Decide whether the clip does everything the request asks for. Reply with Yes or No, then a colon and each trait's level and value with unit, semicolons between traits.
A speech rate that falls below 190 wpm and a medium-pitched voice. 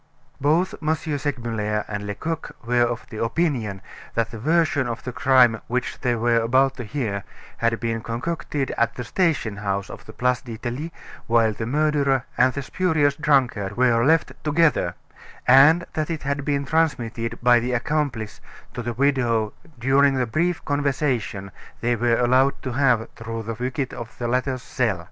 No: average, 165 wpm; low, 125 Hz